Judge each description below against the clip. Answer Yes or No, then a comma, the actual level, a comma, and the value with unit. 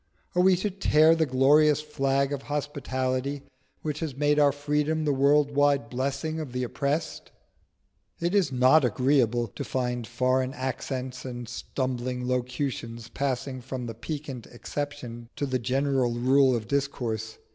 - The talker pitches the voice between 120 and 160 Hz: Yes, low, 135 Hz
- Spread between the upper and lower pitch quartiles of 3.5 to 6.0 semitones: No, average, 2.7 semitones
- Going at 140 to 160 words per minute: Yes, average, 145 wpm